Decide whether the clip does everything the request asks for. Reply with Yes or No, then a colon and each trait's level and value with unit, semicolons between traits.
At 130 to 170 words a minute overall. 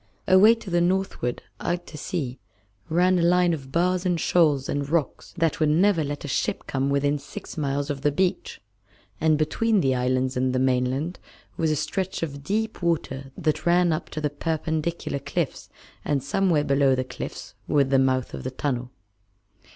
No: average, 180 wpm